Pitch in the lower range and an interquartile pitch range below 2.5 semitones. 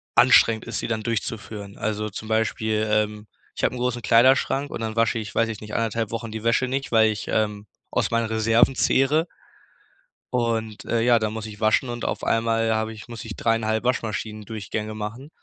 Yes: low, 110 Hz; narrow, 1.4 semitones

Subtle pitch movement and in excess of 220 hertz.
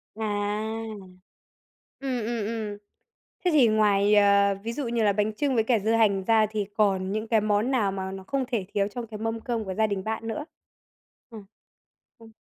No: narrow, 2.1 semitones; high, 215 Hz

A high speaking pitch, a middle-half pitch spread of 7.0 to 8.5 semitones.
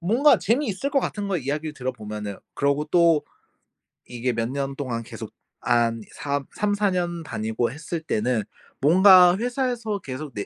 No: medium, 150 Hz; wide, 7.7 semitones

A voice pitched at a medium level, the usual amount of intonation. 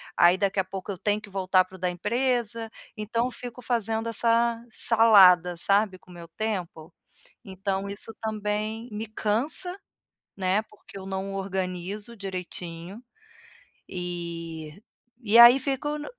No: high, 200 Hz; average, 3.6 semitones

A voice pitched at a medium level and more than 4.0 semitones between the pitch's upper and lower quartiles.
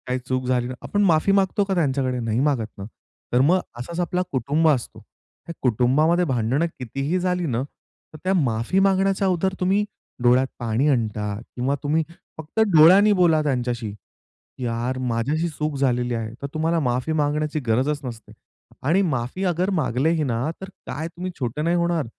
Yes: medium, 145 Hz; wide, 5.6 semitones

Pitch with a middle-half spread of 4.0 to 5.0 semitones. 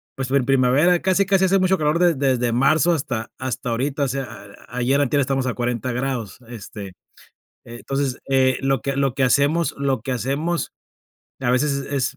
No: narrow, 2.5 semitones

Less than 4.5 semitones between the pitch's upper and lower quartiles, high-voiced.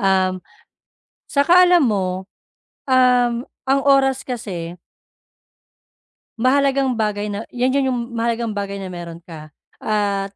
No: average, 5.1 semitones; high, 225 Hz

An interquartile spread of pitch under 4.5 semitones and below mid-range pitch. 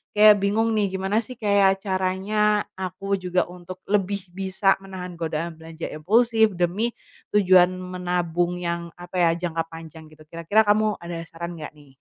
No: average, 2.9 semitones; medium, 185 Hz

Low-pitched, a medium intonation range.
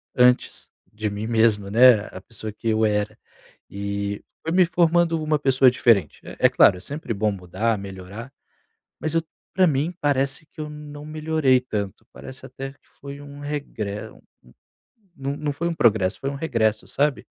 No: low, 130 Hz; wide, 5.9 semitones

